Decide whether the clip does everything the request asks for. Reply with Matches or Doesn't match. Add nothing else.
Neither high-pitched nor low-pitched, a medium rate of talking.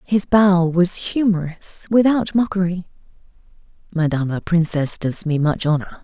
Doesn't match